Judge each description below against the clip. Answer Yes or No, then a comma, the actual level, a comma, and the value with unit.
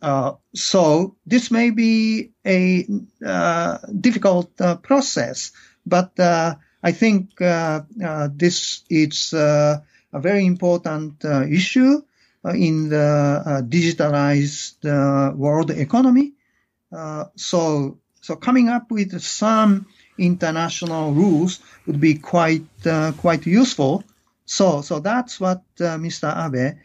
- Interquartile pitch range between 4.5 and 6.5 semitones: Yes, average, 4.8 semitones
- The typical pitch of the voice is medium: Yes, medium, 175 Hz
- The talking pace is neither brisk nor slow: No, slow, 120 wpm